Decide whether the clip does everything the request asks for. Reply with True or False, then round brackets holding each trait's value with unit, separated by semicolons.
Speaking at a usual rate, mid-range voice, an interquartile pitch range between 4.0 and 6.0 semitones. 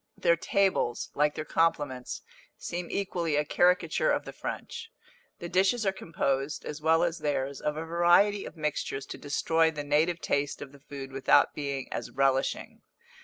False (170 wpm; 155 Hz; 3.5 semitones)